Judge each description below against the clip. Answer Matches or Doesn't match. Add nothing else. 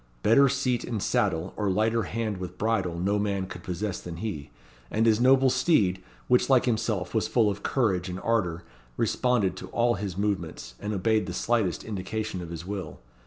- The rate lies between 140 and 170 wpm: Doesn't match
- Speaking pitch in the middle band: Doesn't match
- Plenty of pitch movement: Doesn't match